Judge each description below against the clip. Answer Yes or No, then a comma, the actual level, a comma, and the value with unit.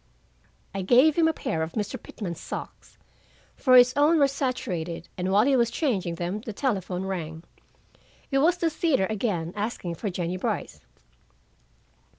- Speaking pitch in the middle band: No, high, 210 Hz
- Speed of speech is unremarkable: Yes, average, 160 wpm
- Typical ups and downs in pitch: No, wide, 7.1 semitones